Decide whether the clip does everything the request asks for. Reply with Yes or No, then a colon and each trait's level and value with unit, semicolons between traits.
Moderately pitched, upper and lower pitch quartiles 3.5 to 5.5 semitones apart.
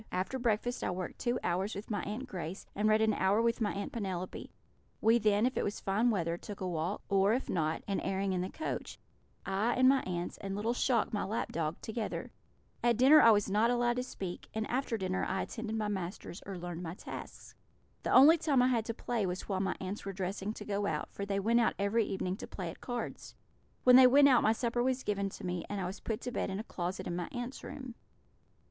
No: high, 205 Hz; average, 4.0 semitones